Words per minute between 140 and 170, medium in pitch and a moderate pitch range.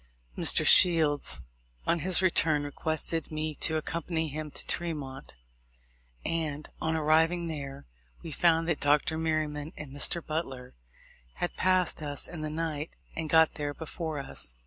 No: average, 145 wpm; medium, 155 Hz; narrow, 2.0 semitones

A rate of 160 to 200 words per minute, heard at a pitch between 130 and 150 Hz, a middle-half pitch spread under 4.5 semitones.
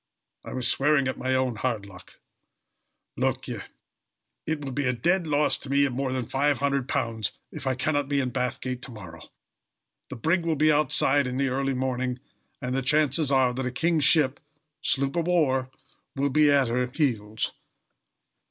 Yes: average, 180 wpm; low, 135 Hz; narrow, 2.4 semitones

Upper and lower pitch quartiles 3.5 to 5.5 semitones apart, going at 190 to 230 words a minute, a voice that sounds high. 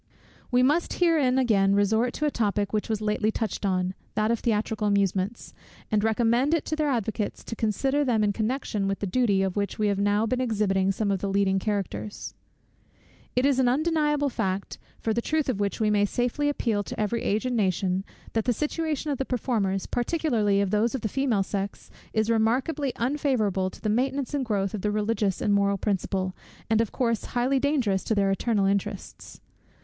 Yes: average, 4.1 semitones; average, 195 wpm; high, 220 Hz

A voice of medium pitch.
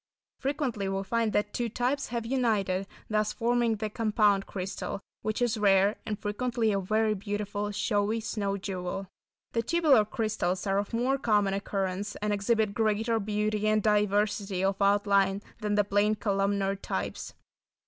No: high, 210 Hz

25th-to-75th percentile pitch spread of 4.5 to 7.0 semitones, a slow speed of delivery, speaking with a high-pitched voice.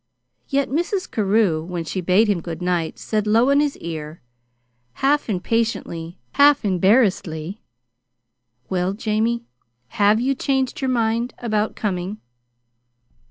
Yes: average, 5.2 semitones; slow, 120 wpm; high, 215 Hz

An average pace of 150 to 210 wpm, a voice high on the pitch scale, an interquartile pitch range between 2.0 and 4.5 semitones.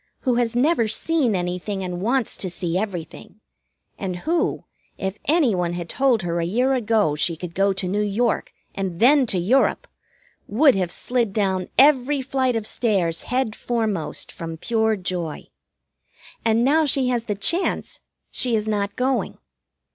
No: average, 160 wpm; high, 215 Hz; wide, 5.5 semitones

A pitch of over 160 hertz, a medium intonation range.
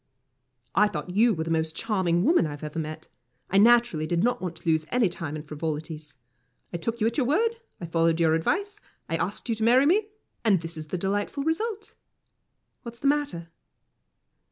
No: medium, 185 Hz; wide, 7.0 semitones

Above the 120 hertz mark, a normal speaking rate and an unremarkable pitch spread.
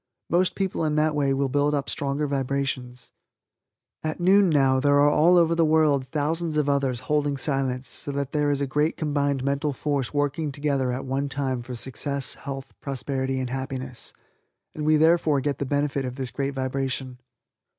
No: medium, 140 Hz; average, 180 wpm; narrow, 2.0 semitones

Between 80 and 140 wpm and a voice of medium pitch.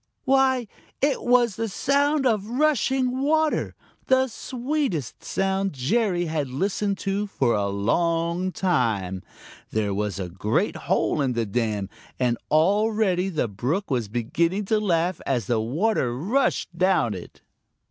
Yes: slow, 135 wpm; medium, 180 Hz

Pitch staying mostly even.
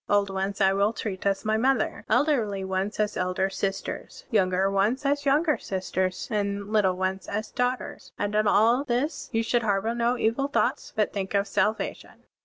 No: average, 3.4 semitones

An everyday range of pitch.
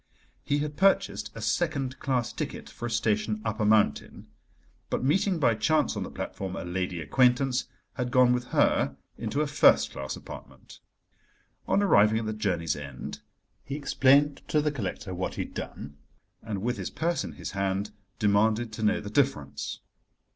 No: wide, 5.7 semitones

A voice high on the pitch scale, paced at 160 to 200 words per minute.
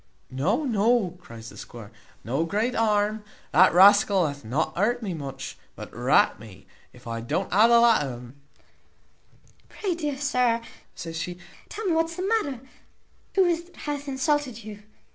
Yes: high, 210 Hz; average, 170 wpm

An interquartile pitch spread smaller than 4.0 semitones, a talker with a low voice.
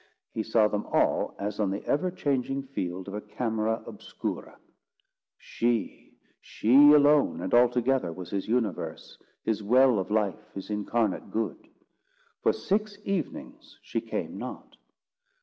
No: average, 4.3 semitones; low, 110 Hz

